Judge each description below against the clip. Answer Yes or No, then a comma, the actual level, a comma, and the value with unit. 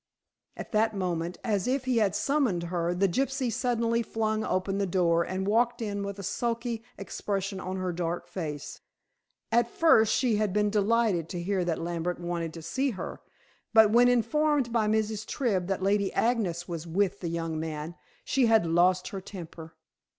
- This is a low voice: No, high, 200 Hz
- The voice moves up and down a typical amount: Yes, average, 4.7 semitones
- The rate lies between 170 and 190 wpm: Yes, average, 180 wpm